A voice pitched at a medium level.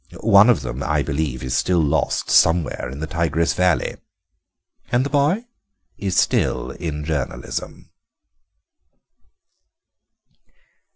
No: very low, 80 Hz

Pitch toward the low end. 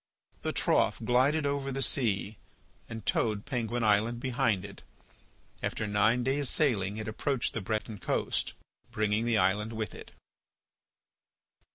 Yes: low, 115 Hz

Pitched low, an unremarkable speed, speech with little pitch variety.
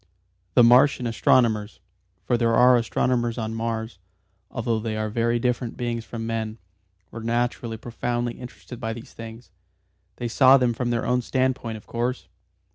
Yes: low, 115 Hz; average, 155 wpm; narrow, 1.4 semitones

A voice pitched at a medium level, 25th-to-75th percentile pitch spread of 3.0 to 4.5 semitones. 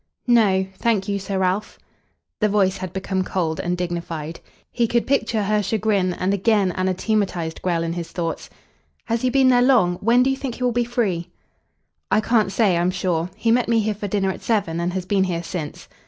No: high, 195 Hz; average, 4.1 semitones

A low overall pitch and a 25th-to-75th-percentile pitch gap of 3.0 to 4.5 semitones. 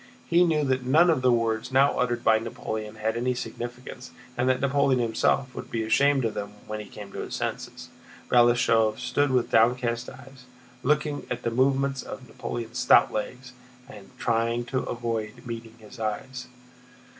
No: low, 120 Hz; narrow, 2.5 semitones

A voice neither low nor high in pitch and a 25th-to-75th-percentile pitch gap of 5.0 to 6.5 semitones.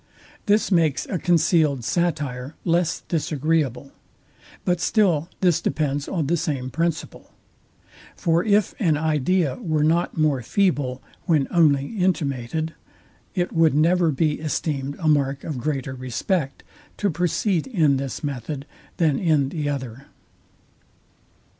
No: medium, 155 Hz; average, 3.7 semitones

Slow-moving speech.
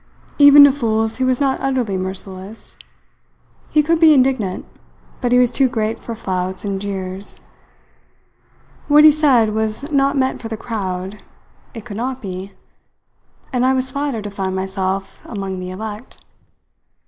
No: average, 155 wpm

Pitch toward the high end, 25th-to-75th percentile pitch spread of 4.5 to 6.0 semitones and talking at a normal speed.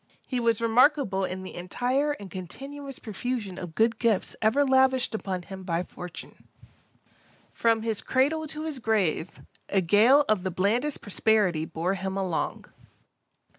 Yes: high, 220 Hz; wide, 5.6 semitones; average, 145 wpm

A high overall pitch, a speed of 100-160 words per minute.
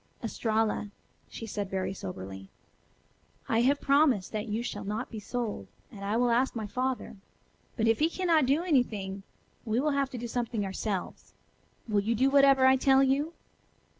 No: high, 235 Hz; average, 170 wpm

